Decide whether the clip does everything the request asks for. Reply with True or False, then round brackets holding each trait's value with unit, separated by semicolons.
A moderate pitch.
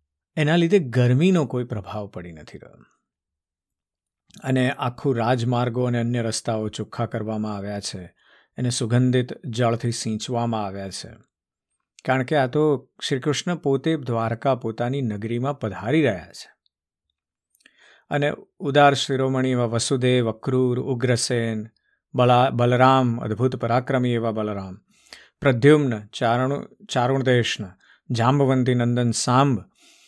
False (120 Hz)